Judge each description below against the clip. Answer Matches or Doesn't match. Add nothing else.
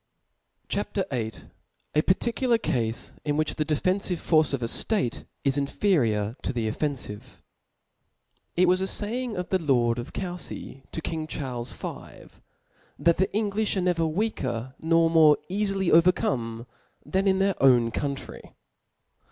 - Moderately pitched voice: Matches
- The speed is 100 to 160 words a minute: Matches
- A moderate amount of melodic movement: Doesn't match